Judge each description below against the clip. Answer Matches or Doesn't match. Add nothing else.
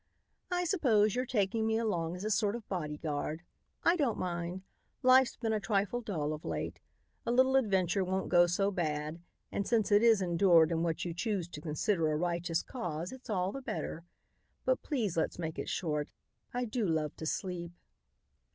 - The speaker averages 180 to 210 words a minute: Matches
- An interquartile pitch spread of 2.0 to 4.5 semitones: Doesn't match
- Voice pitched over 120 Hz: Matches